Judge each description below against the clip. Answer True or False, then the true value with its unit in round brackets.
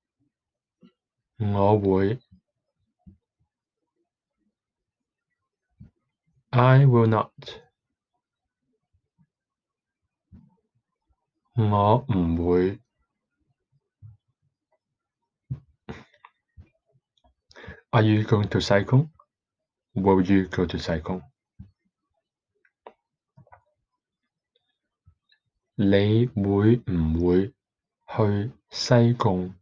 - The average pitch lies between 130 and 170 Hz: False (105 Hz)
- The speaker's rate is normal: False (40 wpm)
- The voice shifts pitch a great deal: False (4.3 semitones)